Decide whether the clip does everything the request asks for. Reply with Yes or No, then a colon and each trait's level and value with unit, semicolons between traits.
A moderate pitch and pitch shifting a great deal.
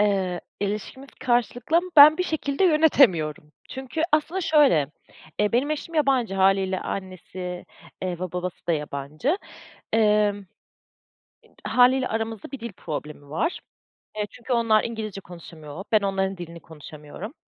No: high, 210 Hz; wide, 6.7 semitones